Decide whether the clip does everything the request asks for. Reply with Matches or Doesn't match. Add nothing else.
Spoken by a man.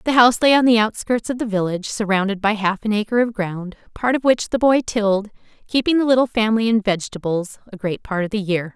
Doesn't match